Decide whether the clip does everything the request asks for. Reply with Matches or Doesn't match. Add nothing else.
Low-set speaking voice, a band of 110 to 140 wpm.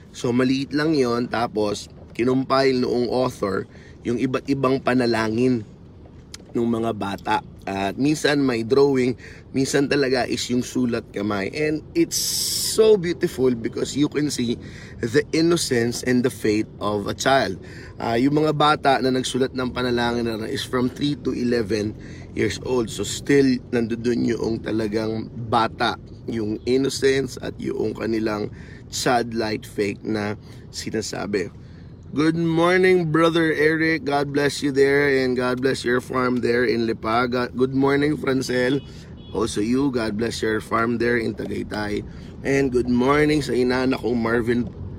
Doesn't match